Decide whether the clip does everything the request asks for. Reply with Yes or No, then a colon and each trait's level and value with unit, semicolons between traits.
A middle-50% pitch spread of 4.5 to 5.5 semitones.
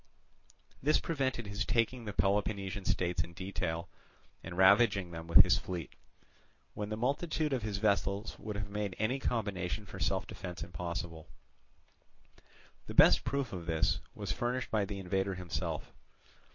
No: average, 3.6 semitones